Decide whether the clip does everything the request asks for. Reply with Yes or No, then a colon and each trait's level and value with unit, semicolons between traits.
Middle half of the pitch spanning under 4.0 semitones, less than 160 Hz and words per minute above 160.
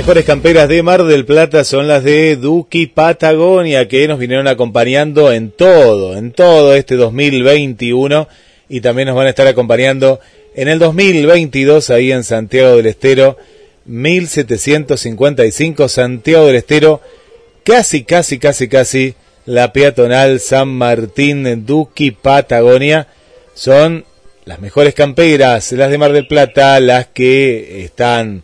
No: average, 3.5 semitones; medium, 140 Hz; average, 135 wpm